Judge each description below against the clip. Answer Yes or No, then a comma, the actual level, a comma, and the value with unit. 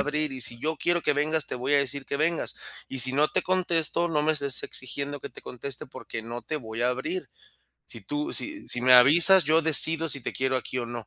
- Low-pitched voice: No, medium, 145 Hz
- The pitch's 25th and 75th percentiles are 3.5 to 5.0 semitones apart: Yes, average, 4.0 semitones